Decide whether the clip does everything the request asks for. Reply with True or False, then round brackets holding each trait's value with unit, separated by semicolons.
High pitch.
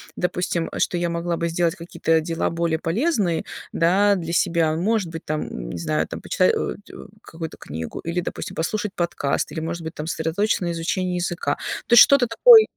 False (170 Hz)